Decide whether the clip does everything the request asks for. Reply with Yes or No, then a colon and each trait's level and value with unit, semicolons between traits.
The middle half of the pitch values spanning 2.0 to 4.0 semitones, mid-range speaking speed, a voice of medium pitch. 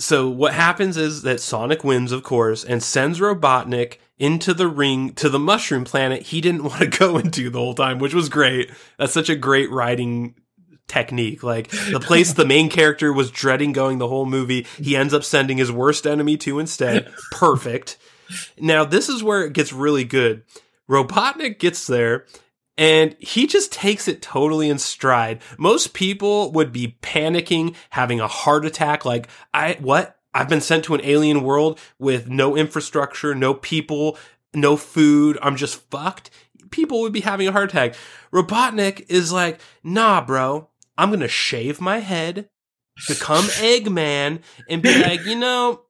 No: average, 4.7 semitones; average, 175 wpm; medium, 150 Hz